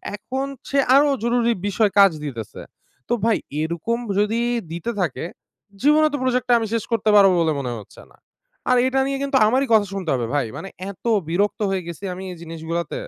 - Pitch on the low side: No, high, 210 Hz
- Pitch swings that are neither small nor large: No, wide, 6.6 semitones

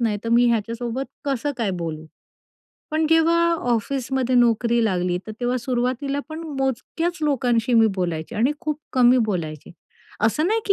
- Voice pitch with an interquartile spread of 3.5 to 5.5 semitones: Yes, average, 4.1 semitones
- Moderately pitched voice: No, high, 240 Hz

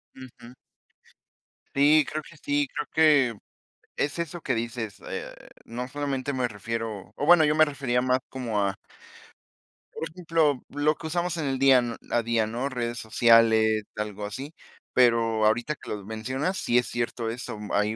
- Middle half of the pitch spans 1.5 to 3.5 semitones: No, average, 4.3 semitones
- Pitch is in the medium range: No, low, 125 Hz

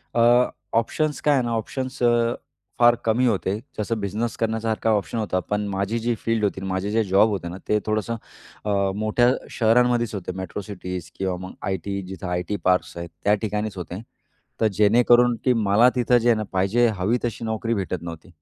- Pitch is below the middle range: Yes, low, 110 Hz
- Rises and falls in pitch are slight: No, average, 3.5 semitones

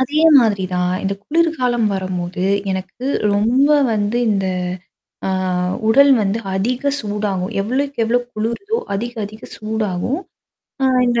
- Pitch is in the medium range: No, high, 220 Hz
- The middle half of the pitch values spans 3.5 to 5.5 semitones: Yes, average, 4.5 semitones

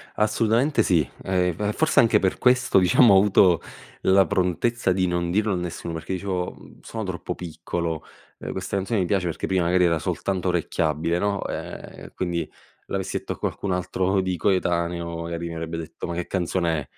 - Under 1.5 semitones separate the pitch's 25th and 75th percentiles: No, narrow, 2.4 semitones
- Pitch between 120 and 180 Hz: No, very low, 90 Hz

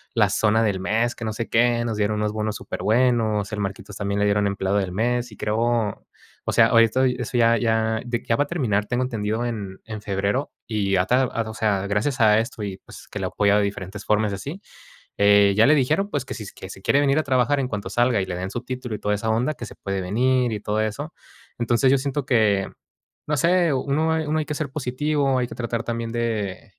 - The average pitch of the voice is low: Yes, low, 115 Hz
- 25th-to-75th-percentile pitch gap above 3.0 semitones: Yes, average, 3.7 semitones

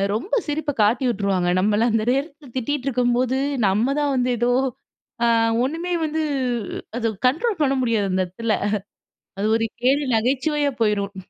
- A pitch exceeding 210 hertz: Yes, very high, 250 Hz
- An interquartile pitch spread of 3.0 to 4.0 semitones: No, average, 4.8 semitones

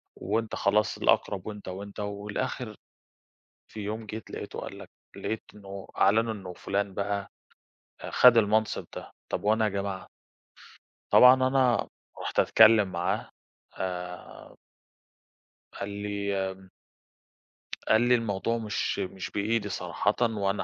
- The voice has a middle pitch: No, low, 105 Hz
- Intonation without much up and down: Yes, narrow, 2.1 semitones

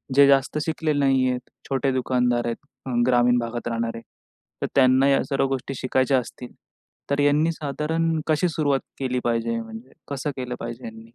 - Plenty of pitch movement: No, average, 2.7 semitones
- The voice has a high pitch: No, low, 130 Hz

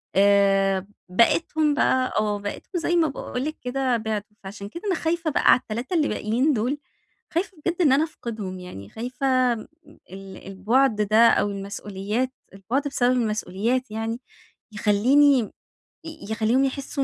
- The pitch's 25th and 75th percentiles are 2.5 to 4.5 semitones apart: No, average, 5.0 semitones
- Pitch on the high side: Yes, high, 235 Hz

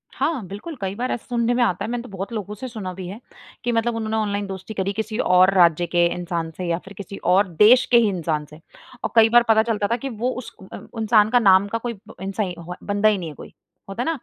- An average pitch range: Yes, average, 3.7 semitones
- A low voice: No, high, 205 Hz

